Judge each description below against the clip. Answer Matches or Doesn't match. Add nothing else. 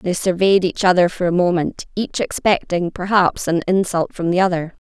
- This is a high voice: Doesn't match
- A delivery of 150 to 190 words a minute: Matches